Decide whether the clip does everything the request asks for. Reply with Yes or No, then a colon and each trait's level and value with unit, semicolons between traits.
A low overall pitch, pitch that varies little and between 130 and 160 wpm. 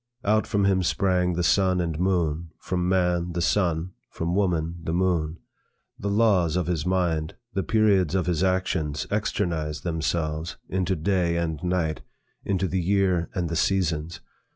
Yes: very low, 90 Hz; narrow, 2.3 semitones; average, 155 wpm